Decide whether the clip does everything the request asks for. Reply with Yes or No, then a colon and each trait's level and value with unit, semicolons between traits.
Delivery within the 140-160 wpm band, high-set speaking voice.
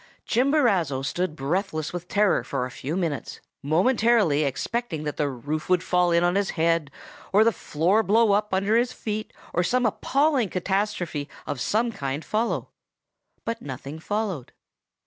No: average, 155 wpm; medium, 180 Hz